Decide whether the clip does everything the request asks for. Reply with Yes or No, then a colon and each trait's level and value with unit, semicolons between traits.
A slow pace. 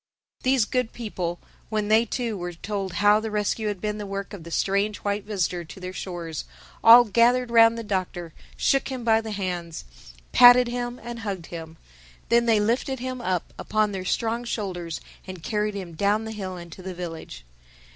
No: average, 185 wpm